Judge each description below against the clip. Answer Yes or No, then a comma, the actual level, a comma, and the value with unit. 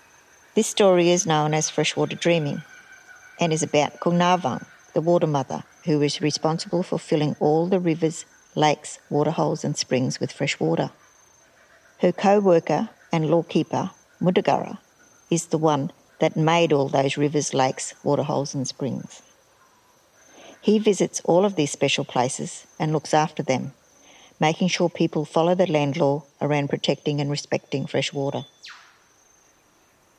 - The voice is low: No, medium, 160 Hz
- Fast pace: No, average, 140 wpm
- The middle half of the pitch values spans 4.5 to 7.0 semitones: No, average, 3.0 semitones